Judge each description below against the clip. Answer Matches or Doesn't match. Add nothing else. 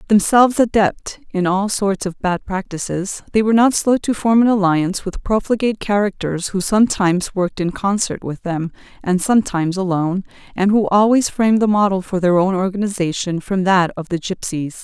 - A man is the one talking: Doesn't match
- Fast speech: Doesn't match